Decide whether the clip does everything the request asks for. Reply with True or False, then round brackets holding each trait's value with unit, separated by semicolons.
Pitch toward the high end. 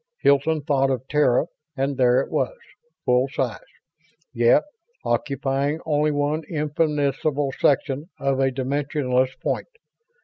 False (140 Hz)